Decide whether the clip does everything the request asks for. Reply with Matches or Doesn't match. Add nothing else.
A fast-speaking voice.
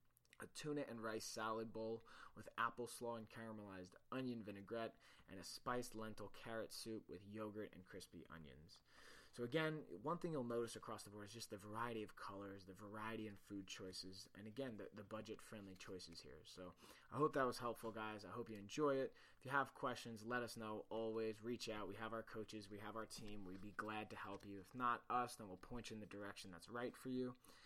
Matches